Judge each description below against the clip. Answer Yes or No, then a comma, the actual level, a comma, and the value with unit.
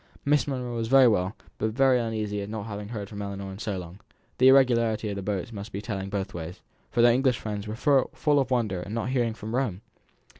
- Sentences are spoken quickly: Yes, fast, 230 wpm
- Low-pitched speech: Yes, low, 110 Hz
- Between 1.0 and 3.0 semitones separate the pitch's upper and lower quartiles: No, average, 3.5 semitones